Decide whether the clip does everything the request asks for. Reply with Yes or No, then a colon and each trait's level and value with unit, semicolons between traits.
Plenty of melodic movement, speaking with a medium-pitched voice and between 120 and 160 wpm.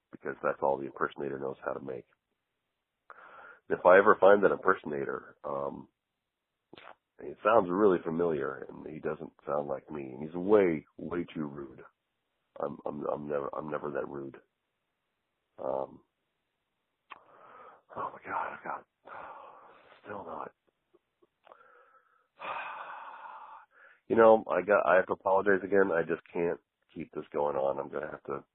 No: wide, 6.0 semitones; very low, 75 Hz; average, 145 wpm